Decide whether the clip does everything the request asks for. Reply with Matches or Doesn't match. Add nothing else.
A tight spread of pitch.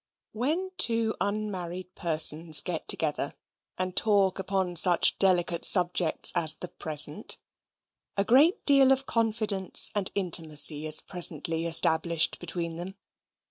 Doesn't match